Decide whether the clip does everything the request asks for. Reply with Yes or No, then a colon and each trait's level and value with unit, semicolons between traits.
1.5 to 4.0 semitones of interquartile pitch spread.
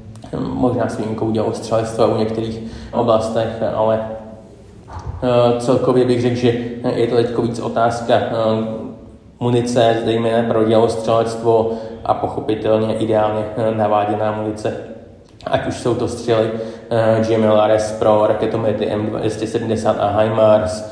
No: narrow, 1.1 semitones